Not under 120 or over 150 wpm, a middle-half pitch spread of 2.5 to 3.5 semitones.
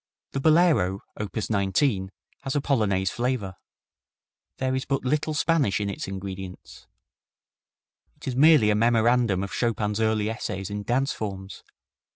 No: average, 140 wpm; average, 5.3 semitones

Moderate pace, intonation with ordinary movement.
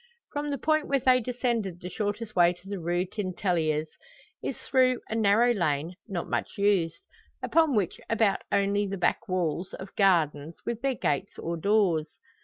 Yes: average, 170 wpm; average, 4.9 semitones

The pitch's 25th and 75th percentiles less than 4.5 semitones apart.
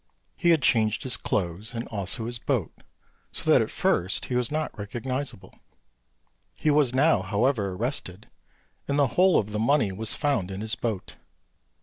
No: wide, 5.6 semitones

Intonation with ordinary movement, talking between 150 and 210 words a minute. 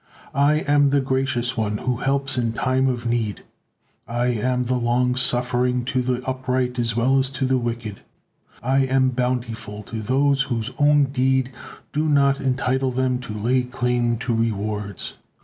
No: narrow, 1.9 semitones; average, 165 wpm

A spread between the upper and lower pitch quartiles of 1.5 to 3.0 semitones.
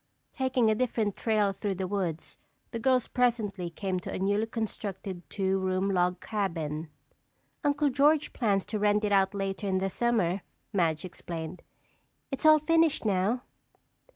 No: average, 3.8 semitones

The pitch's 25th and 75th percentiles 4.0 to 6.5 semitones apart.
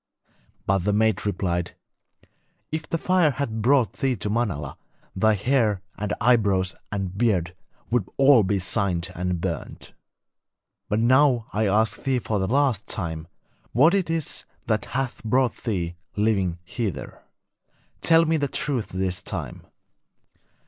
Yes: wide, 5.5 semitones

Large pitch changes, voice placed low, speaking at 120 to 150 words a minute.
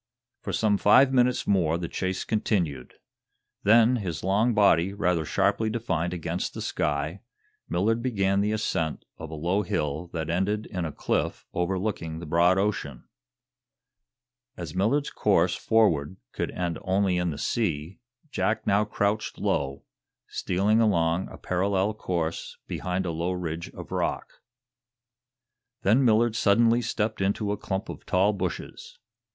No: average, 4.0 semitones; very low, 95 Hz; average, 145 wpm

